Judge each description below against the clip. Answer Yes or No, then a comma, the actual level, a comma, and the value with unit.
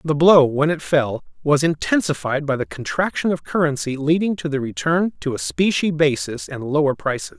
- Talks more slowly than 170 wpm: No, average, 185 wpm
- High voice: No, medium, 150 Hz